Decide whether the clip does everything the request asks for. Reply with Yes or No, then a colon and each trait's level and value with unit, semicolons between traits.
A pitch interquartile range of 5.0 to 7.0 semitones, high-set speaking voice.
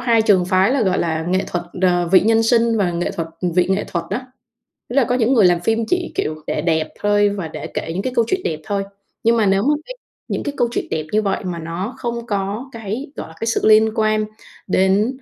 No: average, 4.3 semitones; high, 205 Hz